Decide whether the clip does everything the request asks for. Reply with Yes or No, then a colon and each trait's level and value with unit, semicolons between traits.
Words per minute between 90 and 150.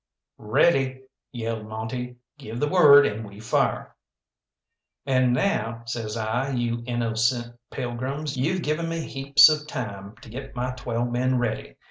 Yes: average, 140 wpm